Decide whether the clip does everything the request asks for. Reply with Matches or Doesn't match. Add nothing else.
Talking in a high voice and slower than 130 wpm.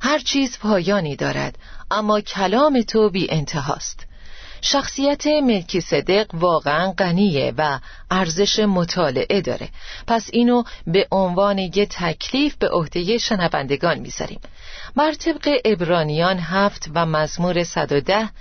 Matches